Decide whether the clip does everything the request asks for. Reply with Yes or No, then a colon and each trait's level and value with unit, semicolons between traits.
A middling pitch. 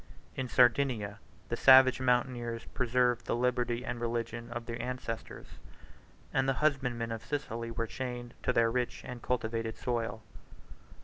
No: low, 120 Hz